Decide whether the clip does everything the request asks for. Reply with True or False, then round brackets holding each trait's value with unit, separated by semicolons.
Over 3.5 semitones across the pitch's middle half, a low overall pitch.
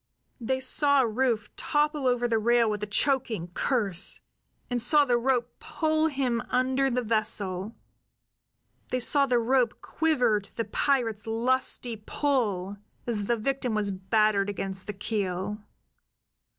False (3.9 semitones; 235 Hz)